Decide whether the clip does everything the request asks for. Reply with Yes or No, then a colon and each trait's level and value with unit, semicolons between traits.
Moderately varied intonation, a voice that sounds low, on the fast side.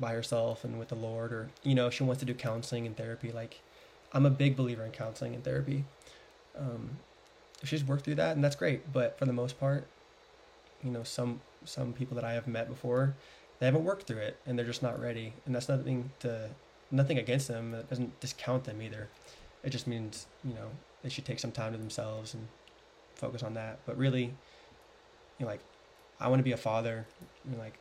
Yes: average, 3.0 semitones; low, 125 Hz; fast, 220 wpm